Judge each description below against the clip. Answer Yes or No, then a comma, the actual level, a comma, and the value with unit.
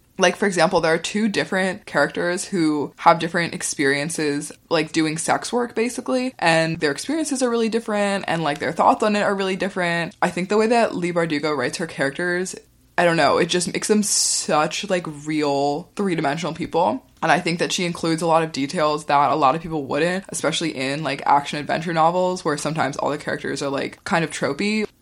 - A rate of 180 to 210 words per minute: Yes, fast, 205 wpm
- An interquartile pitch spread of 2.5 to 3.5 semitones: No, average, 4.3 semitones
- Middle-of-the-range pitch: Yes, medium, 170 Hz